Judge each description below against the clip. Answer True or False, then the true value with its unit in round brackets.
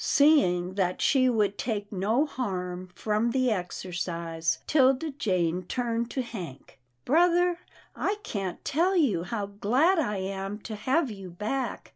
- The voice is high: True (210 Hz)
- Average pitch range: False (6.5 semitones)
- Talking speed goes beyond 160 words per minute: False (145 wpm)